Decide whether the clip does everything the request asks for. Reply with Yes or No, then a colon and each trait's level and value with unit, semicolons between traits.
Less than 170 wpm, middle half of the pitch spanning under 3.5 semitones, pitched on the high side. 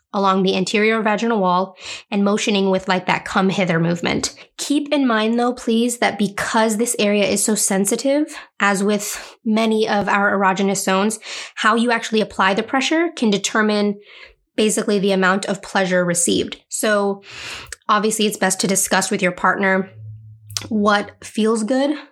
Yes: average, 155 wpm; average, 2.7 semitones; high, 205 Hz